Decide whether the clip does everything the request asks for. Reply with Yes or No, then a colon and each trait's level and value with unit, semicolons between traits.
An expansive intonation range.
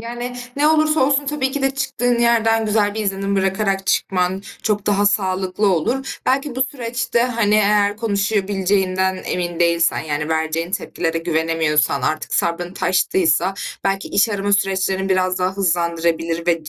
No: average, 4.5 semitones